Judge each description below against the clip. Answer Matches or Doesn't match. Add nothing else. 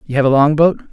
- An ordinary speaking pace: Doesn't match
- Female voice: Doesn't match